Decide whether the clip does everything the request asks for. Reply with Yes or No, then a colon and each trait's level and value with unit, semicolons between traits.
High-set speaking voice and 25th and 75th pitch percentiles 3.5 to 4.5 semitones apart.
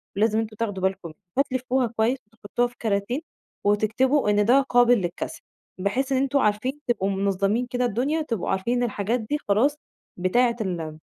Yes: high, 225 Hz; average, 3.9 semitones